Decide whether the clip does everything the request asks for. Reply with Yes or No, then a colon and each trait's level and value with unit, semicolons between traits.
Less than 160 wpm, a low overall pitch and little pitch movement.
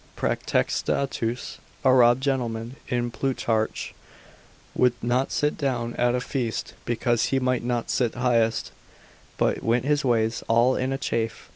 Yes: average, 140 wpm; low, 120 Hz; narrow, 2.0 semitones